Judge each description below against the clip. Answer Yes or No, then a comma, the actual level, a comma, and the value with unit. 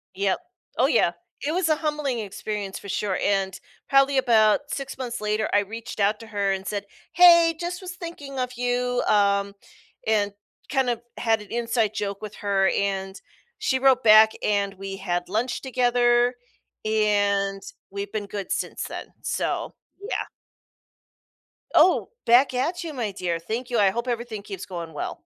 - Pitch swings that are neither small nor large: Yes, average, 4.2 semitones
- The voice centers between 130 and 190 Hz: No, high, 220 Hz